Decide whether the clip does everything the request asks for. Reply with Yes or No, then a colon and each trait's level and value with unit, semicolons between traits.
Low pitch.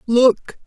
No: high, 240 Hz